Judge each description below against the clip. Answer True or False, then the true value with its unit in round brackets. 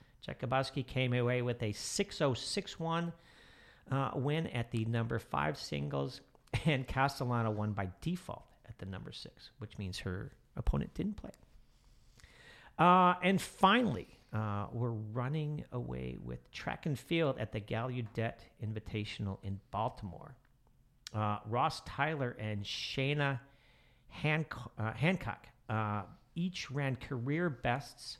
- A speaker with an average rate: False (130 wpm)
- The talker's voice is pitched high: False (125 Hz)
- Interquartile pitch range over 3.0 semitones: True (4.6 semitones)